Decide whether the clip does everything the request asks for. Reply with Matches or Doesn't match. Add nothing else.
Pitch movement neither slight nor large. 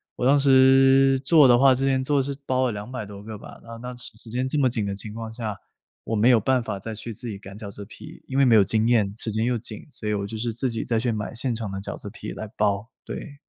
Matches